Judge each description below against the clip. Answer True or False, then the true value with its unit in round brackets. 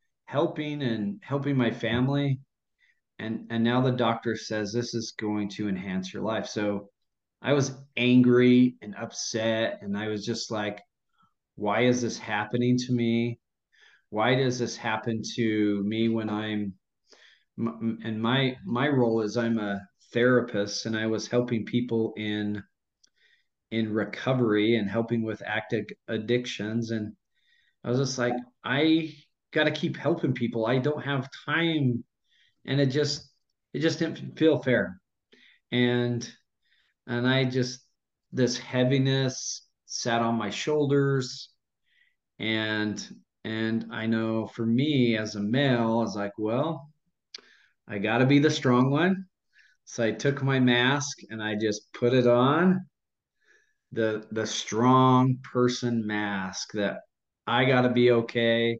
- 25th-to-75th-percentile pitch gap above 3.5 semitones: False (3.2 semitones)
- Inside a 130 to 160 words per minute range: True (140 wpm)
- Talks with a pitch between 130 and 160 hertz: False (120 Hz)